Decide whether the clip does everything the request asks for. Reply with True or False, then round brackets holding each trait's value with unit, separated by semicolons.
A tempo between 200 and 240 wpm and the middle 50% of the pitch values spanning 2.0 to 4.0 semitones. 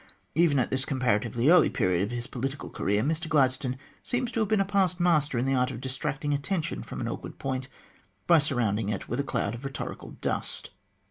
False (205 wpm; 4.7 semitones)